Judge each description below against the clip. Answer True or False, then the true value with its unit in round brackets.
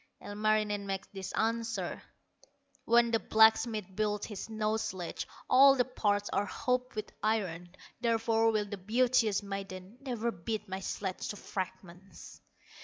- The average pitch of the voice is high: True (215 Hz)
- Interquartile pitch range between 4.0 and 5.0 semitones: False (2.5 semitones)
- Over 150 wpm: False (135 wpm)